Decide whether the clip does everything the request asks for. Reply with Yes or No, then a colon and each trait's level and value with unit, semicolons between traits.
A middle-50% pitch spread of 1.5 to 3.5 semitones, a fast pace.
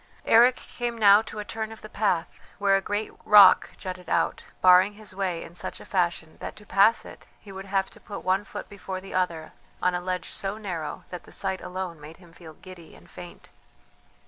Yes: narrow, 2.4 semitones; fast, 215 wpm